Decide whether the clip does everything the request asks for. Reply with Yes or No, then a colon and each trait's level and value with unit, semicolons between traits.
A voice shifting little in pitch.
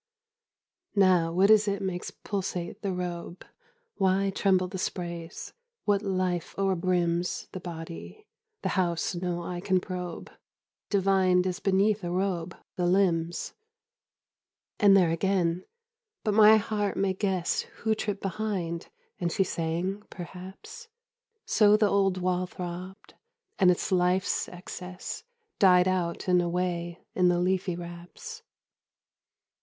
Yes: narrow, 1.9 semitones